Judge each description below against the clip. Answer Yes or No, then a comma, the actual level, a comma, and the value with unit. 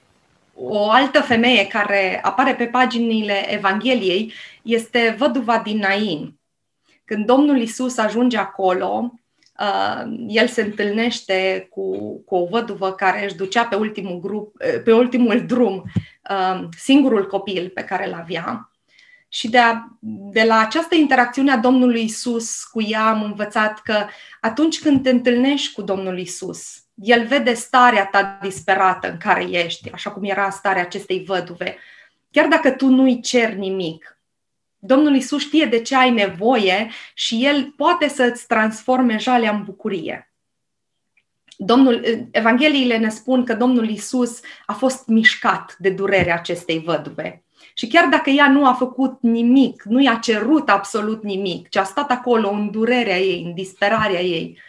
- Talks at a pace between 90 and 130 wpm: No, average, 145 wpm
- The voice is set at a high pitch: Yes, high, 225 Hz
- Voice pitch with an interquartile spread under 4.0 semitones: No, average, 4.3 semitones